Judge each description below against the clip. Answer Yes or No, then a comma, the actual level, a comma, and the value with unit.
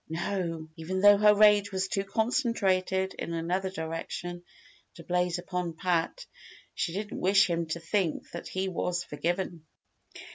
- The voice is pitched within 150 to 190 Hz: Yes, medium, 185 Hz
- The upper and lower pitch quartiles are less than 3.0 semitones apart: Yes, narrow, 2.6 semitones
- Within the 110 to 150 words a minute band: Yes, average, 145 wpm